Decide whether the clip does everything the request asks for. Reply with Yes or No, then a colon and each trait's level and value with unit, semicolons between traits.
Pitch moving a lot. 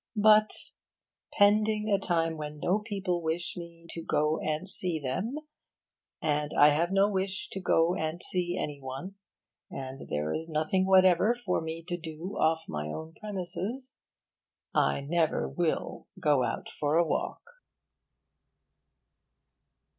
No: average, 3.7 semitones